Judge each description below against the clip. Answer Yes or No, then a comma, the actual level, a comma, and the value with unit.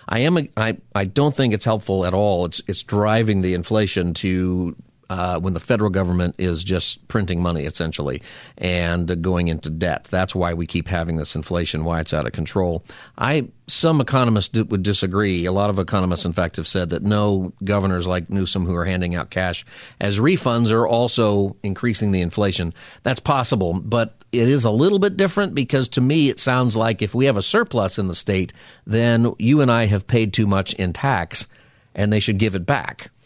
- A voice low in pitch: Yes, low, 100 Hz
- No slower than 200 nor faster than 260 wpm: Yes, fast, 205 wpm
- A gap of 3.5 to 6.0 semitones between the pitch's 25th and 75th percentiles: Yes, average, 4.4 semitones